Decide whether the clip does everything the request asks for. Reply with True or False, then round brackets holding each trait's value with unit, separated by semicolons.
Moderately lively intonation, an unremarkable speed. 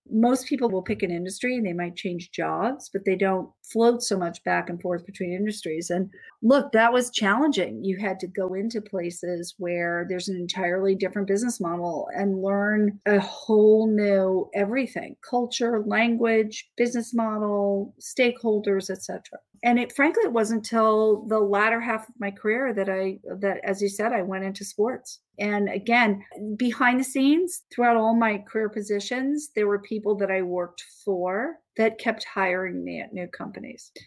True (3.4 semitones; 175 wpm)